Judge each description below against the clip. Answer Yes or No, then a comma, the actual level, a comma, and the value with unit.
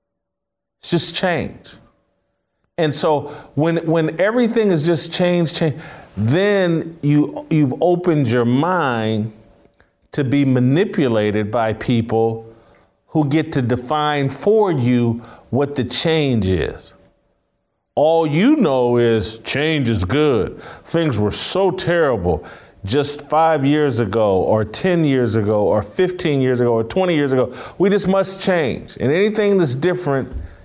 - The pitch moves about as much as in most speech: No, wide, 6.5 semitones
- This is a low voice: No, medium, 145 Hz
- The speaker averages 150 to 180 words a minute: No, slow, 135 wpm